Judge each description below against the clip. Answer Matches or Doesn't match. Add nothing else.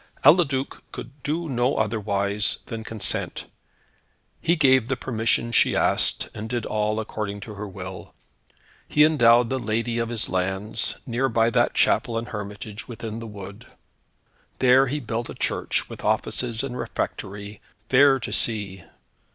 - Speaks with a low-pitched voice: Matches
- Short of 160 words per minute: Matches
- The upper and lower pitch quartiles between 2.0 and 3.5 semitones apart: Matches